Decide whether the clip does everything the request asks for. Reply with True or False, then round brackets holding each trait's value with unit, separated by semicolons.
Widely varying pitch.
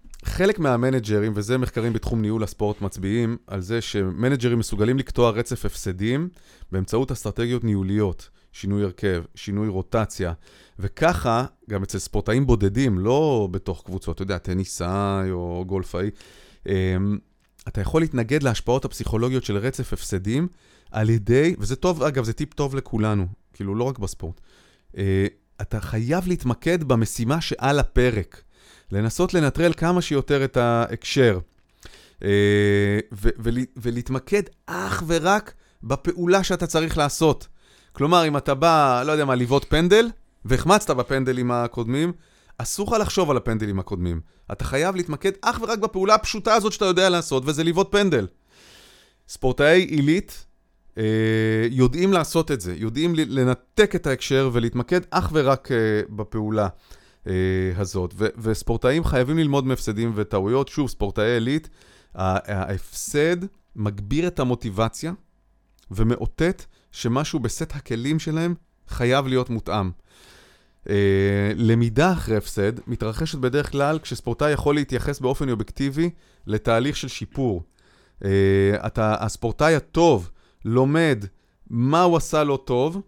True (6.4 semitones)